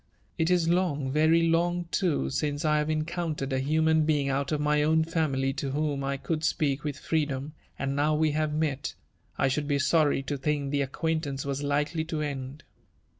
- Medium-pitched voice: Yes, medium, 150 Hz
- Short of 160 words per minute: No, average, 200 wpm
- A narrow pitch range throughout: Yes, narrow, 2.2 semitones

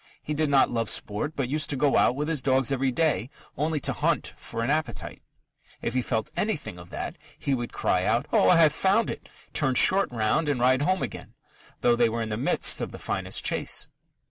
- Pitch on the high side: No, low, 135 Hz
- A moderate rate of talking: No, fast, 220 wpm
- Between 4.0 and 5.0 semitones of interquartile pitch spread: Yes, average, 4.4 semitones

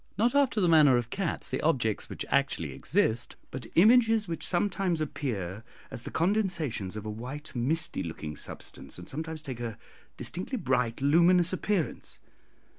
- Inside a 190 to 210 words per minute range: No, average, 155 wpm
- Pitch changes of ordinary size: No, wide, 7.4 semitones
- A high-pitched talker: No, medium, 155 Hz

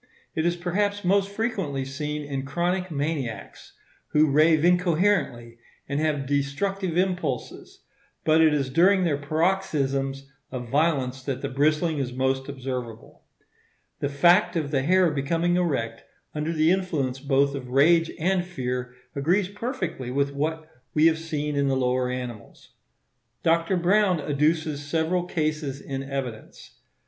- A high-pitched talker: No, medium, 150 Hz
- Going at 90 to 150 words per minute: Yes, average, 140 wpm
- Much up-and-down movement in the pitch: No, average, 4.1 semitones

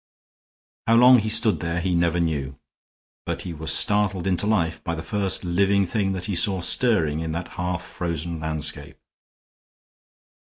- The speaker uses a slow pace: No, average, 160 wpm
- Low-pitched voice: Yes, very low, 90 Hz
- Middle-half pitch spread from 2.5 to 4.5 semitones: Yes, average, 3.6 semitones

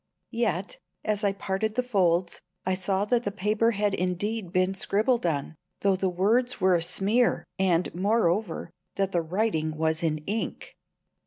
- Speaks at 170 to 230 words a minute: No, average, 160 wpm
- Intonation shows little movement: No, average, 3.6 semitones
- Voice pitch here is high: Yes, high, 195 Hz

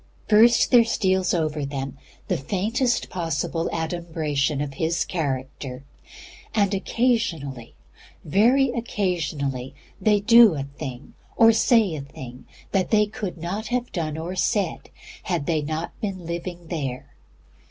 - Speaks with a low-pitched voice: No, medium, 170 Hz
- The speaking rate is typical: No, slow, 130 wpm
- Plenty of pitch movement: Yes, wide, 6.4 semitones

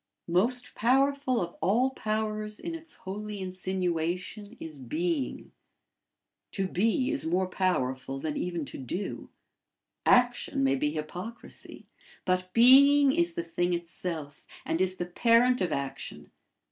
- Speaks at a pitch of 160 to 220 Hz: Yes, medium, 185 Hz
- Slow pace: Yes, slow, 130 wpm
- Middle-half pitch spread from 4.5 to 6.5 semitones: Yes, wide, 5.6 semitones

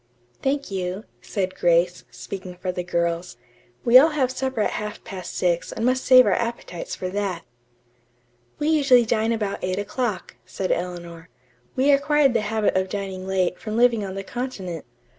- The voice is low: No, high, 200 Hz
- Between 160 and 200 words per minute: Yes, average, 170 wpm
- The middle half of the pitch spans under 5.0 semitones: No, average, 5.3 semitones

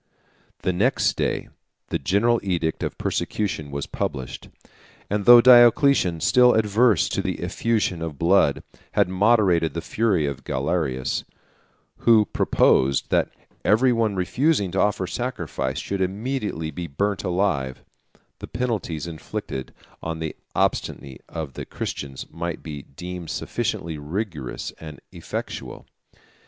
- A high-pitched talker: No, very low, 90 Hz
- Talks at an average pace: No, slow, 130 wpm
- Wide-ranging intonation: Yes, wide, 5.7 semitones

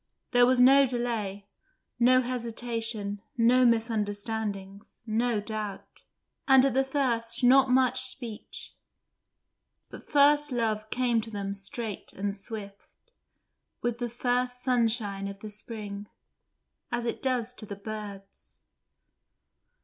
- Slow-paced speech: Yes, slow, 120 wpm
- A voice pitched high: Yes, high, 230 Hz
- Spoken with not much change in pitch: No, average, 3.2 semitones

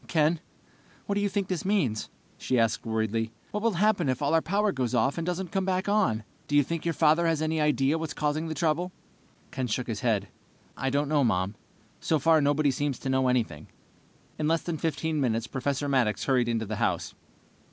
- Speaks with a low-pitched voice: No, medium, 145 Hz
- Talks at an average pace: No, fast, 210 wpm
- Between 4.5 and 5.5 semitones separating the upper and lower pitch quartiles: Yes, average, 5.0 semitones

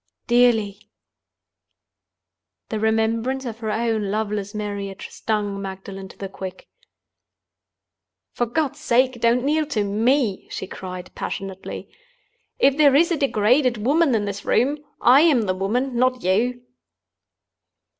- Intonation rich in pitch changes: No, average, 4.1 semitones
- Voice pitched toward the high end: Yes, high, 225 Hz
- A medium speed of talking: No, slow, 125 wpm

